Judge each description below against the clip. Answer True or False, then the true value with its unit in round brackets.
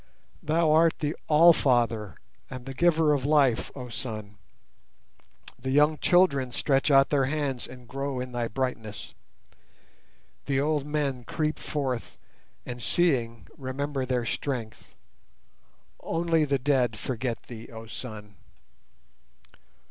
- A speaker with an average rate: False (125 wpm)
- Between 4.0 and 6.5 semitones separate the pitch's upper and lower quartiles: False (3.6 semitones)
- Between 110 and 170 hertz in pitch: True (135 Hz)